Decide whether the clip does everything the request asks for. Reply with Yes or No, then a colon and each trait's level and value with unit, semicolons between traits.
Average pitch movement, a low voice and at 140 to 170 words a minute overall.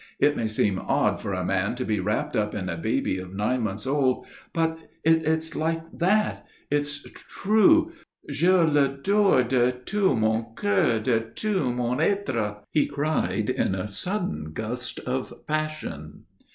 No: wide, 7.2 semitones; low, 130 Hz; average, 150 wpm